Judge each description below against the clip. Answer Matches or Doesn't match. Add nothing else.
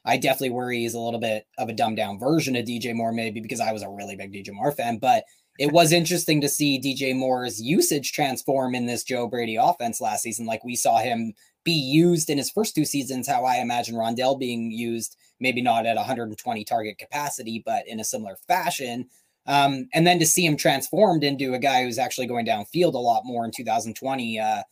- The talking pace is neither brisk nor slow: Doesn't match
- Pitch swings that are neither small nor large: Matches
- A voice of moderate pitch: Doesn't match